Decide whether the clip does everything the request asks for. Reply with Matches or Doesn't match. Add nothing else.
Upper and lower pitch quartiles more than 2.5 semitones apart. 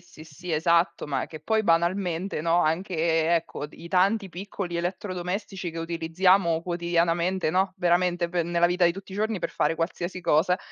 Doesn't match